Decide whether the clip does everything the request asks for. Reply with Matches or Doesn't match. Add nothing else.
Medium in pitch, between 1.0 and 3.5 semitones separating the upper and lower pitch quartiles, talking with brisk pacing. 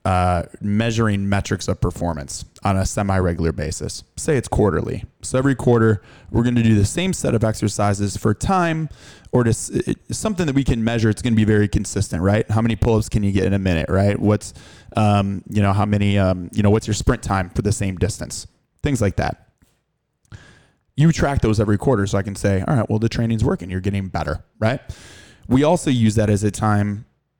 Doesn't match